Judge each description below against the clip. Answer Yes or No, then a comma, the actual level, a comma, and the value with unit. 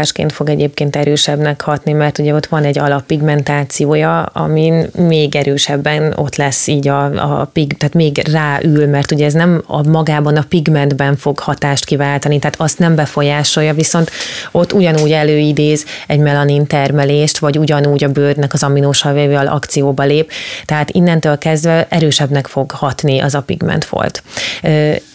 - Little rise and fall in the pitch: Yes, narrow, 1.3 semitones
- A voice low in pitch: No, medium, 150 Hz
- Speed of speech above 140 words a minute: Yes, average, 150 wpm